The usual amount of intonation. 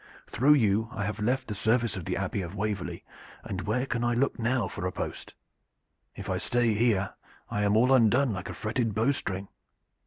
Yes: average, 3.1 semitones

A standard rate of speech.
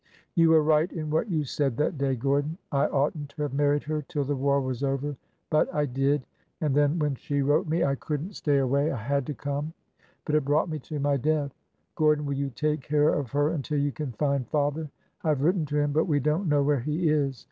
No: fast, 240 wpm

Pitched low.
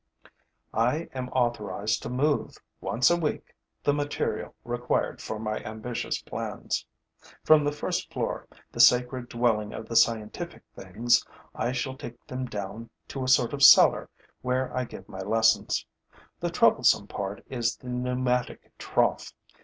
Yes: low, 125 Hz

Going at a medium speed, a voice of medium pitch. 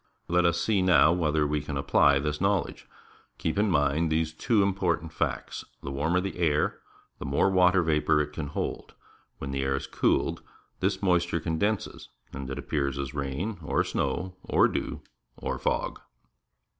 No: average, 170 wpm; very low, 80 Hz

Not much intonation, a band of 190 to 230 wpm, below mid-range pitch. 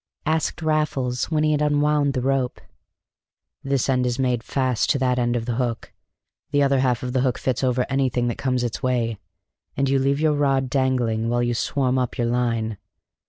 Yes: narrow, 2.2 semitones; average, 200 wpm; low, 130 Hz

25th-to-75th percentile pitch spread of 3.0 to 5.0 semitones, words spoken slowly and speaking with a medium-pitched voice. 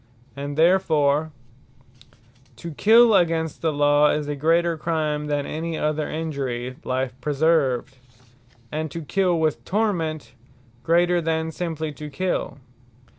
No: narrow, 2.4 semitones; slow, 125 wpm; medium, 155 Hz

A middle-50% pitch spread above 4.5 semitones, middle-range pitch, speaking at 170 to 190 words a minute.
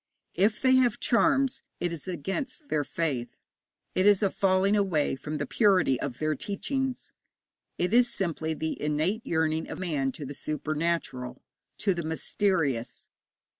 No: average, 5.3 semitones; medium, 170 Hz; average, 150 wpm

